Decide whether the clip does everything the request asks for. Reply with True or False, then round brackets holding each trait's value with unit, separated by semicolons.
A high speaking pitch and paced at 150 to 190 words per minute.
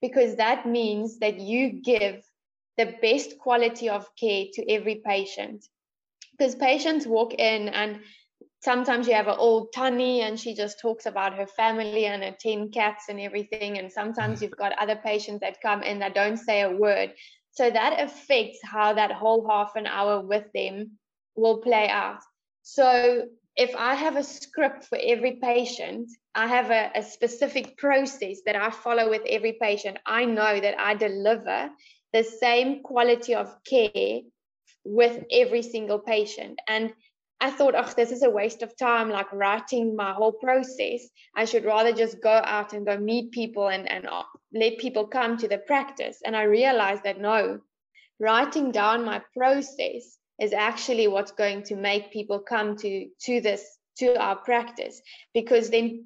True (225 Hz; 170 wpm)